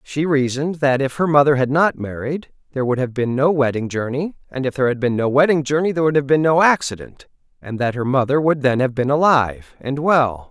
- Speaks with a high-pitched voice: No, medium, 140 Hz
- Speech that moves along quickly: Yes, fast, 235 wpm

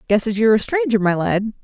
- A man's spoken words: No, female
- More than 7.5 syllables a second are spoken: No, 6.5 syllables/s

